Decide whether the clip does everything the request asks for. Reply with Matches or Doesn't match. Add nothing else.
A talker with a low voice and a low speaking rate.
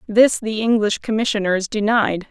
Doesn't match